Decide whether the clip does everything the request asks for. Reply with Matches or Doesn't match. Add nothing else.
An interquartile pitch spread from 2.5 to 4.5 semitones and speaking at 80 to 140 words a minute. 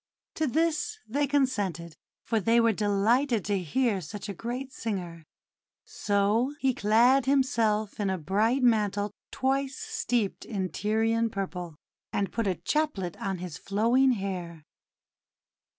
Doesn't match